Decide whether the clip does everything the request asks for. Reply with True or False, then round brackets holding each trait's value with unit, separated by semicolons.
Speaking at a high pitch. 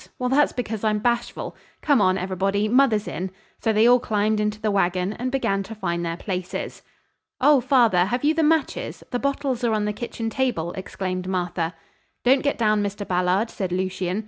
True (210 Hz)